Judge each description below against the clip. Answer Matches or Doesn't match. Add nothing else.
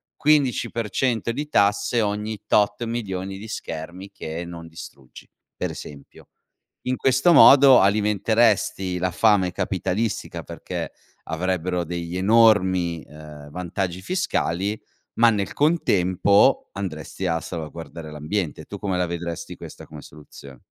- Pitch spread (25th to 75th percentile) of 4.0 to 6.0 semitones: Matches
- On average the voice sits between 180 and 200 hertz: Doesn't match